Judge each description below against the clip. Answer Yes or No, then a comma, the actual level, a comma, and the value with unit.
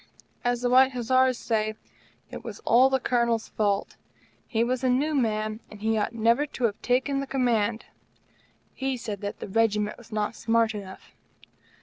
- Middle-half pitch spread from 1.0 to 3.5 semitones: Yes, average, 2.9 semitones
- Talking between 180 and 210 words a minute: No, average, 170 wpm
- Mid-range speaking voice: No, high, 230 Hz